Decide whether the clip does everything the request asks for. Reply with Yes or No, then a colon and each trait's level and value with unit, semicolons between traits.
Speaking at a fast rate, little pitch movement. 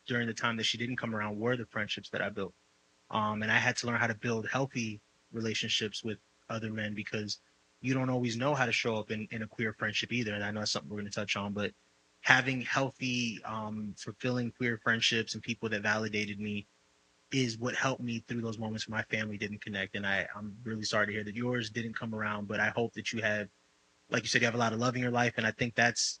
Yes: fast, 255 wpm; narrow, 2.1 semitones